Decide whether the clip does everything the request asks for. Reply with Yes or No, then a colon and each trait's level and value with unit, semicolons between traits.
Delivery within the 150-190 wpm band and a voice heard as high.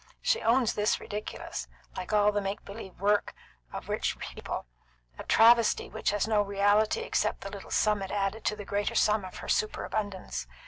Yes: average, 180 wpm; high, 205 Hz